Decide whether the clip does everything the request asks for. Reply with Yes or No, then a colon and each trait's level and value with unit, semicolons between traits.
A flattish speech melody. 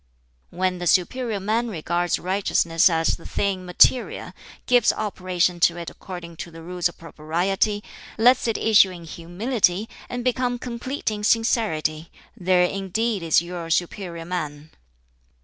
No: average, 4.2 semitones